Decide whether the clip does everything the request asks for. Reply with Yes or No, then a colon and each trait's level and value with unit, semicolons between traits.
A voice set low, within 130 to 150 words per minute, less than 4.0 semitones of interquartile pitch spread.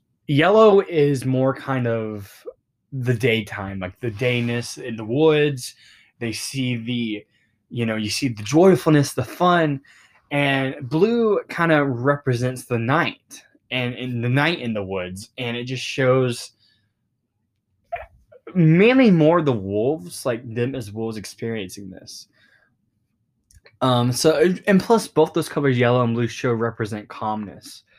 No: low, 125 Hz; average, 140 wpm; average, 4.4 semitones